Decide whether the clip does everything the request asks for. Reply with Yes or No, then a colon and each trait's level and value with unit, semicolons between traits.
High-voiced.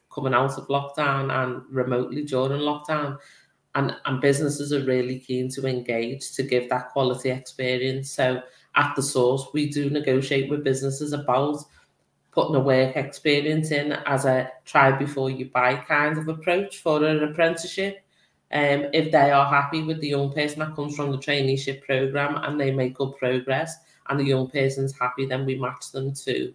No: low, 135 Hz